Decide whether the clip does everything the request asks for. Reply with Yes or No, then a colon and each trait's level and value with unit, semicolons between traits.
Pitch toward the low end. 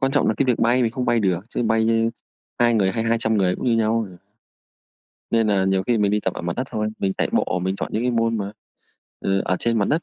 Yes: low, 110 Hz